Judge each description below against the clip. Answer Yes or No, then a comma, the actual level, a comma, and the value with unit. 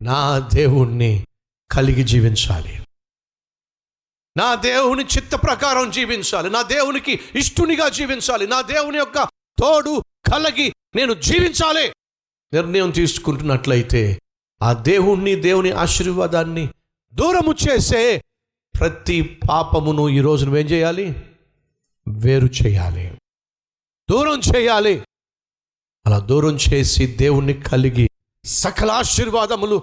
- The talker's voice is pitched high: No, medium, 160 Hz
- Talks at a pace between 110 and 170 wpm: No, average, 90 wpm